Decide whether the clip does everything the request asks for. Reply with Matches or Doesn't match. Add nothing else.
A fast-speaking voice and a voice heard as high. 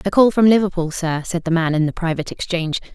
Doesn't match